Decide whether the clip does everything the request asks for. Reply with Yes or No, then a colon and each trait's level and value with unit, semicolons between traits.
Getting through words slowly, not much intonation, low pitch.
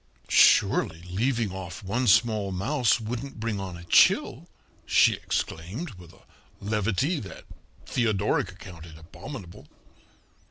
No: slow, 115 wpm; average, 4.5 semitones; low, 100 Hz